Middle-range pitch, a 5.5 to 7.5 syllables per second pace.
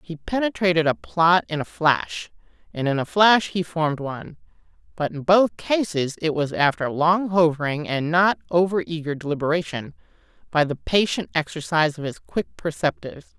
No: medium, 165 Hz; 5.1 syllables/s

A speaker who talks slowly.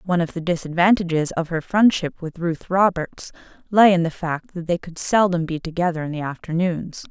No: average, 195 wpm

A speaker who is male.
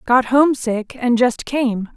No: female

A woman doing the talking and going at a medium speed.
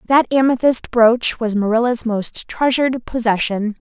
No: female; slow, 125 wpm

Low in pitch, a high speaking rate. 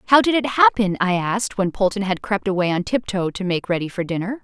No: high, 200 Hz; fast, 255 wpm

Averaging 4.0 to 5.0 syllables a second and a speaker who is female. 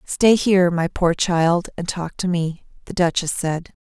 Yes: 4.2 syllables/s; female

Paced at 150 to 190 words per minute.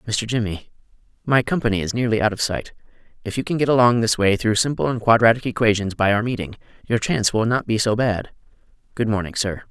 No: average, 200 wpm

